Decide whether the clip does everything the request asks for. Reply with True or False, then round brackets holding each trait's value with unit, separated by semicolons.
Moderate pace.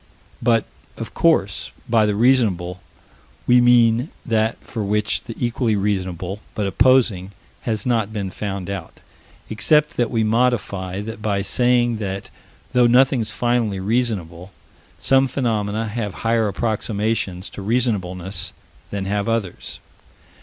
False (125 wpm)